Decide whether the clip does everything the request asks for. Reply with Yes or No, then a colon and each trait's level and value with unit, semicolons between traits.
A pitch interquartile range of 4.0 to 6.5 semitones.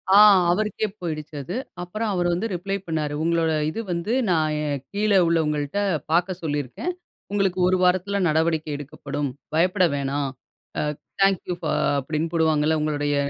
No: average, 3.6 semitones